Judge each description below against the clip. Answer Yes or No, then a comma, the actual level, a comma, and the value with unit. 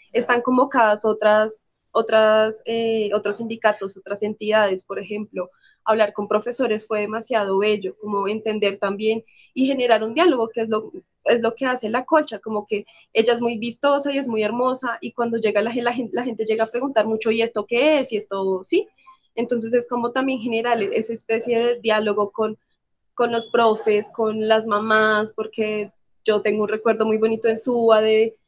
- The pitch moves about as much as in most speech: No, narrow, 1.9 semitones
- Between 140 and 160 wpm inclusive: No, average, 185 wpm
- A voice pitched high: Yes, high, 220 Hz